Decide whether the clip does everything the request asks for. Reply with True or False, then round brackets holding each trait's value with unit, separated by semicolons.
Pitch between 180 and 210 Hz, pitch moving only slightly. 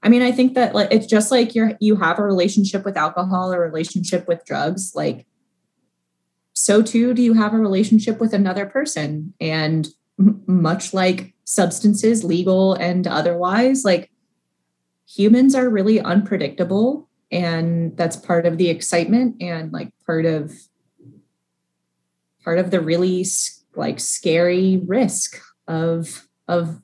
False (185 Hz; 4.3 semitones)